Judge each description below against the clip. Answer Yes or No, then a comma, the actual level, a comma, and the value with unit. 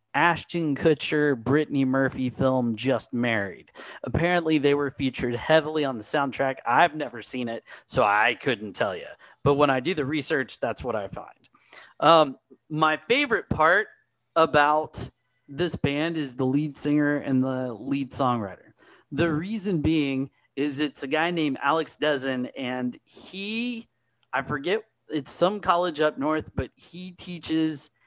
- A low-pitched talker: No, medium, 145 Hz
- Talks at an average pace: Yes, average, 150 wpm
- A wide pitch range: No, average, 3.1 semitones